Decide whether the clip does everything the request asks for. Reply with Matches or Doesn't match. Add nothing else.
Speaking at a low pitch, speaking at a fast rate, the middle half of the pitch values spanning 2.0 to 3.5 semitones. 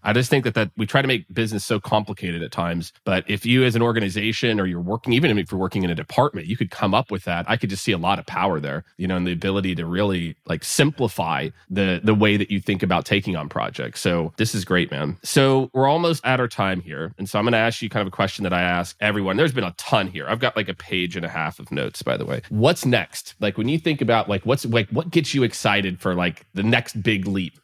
Doesn't match